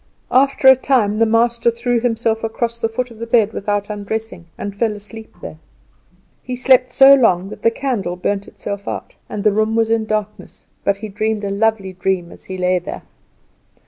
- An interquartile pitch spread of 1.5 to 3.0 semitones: Yes, narrow, 2.5 semitones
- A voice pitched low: No, high, 220 Hz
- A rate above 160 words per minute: Yes, average, 195 wpm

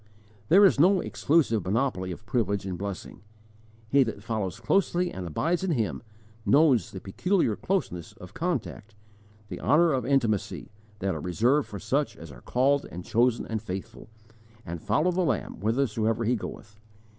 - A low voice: Yes, low, 115 Hz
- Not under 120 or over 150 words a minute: No, average, 160 wpm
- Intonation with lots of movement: Yes, wide, 6.2 semitones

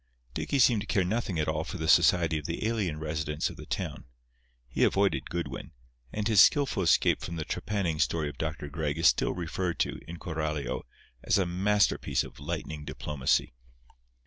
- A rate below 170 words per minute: No, average, 180 wpm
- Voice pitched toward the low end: Yes, very low, 85 Hz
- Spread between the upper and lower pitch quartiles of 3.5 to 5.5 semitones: Yes, average, 4.2 semitones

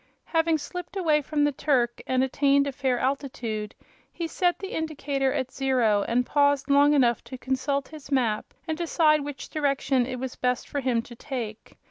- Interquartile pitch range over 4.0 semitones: No, average, 2.9 semitones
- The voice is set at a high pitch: Yes, very high, 275 Hz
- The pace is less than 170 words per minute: No, average, 180 wpm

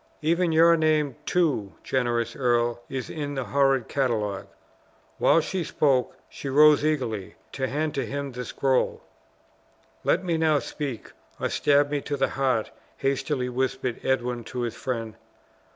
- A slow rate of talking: No, average, 150 wpm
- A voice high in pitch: No, low, 135 Hz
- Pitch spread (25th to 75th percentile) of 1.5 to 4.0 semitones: Yes, average, 3.4 semitones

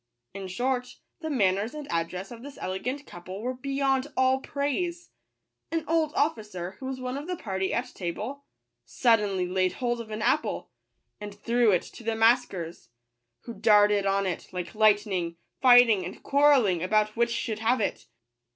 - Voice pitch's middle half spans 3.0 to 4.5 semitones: No, average, 5.2 semitones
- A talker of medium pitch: No, high, 225 Hz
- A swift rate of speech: No, average, 165 wpm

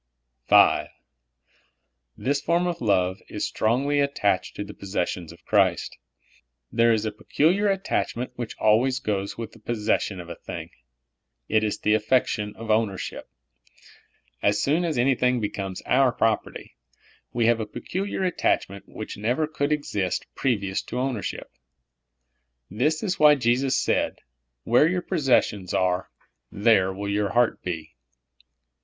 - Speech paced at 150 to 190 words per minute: No, average, 140 wpm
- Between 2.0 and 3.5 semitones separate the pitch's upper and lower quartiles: No, average, 5.3 semitones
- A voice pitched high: No, low, 115 Hz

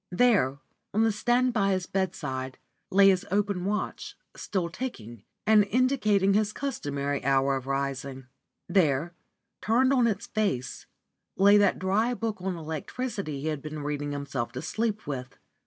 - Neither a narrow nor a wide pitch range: No, wide, 7.3 semitones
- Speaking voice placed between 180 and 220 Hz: Yes, high, 190 Hz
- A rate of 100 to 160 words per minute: Yes, average, 150 wpm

